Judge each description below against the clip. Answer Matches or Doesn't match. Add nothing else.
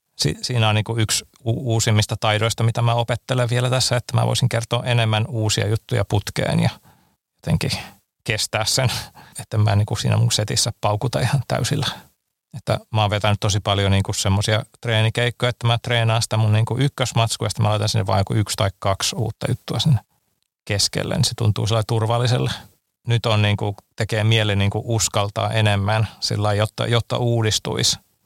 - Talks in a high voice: Doesn't match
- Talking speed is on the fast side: Matches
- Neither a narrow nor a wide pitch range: Doesn't match